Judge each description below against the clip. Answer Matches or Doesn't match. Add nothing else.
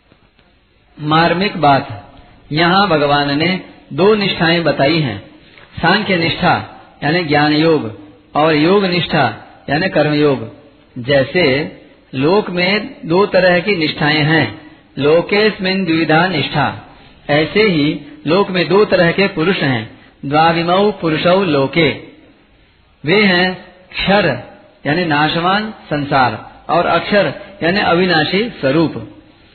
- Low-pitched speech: Doesn't match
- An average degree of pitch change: Matches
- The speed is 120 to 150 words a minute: Doesn't match